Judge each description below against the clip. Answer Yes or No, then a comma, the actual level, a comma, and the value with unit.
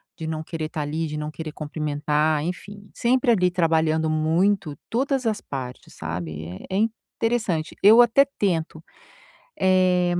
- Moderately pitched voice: Yes, medium, 160 Hz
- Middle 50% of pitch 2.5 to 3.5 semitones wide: No, average, 4.8 semitones